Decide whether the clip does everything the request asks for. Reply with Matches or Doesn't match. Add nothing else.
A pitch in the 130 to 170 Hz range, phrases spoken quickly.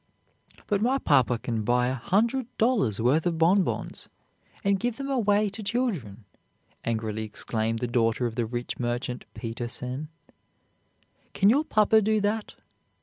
Doesn't match